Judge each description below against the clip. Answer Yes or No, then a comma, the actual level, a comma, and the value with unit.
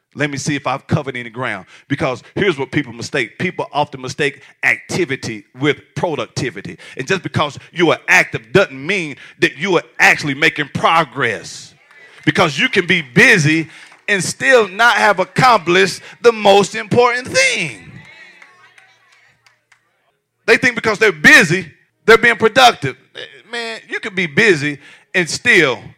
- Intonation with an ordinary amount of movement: No, wide, 7.5 semitones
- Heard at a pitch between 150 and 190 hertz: Yes, medium, 185 Hz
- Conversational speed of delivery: Yes, average, 145 wpm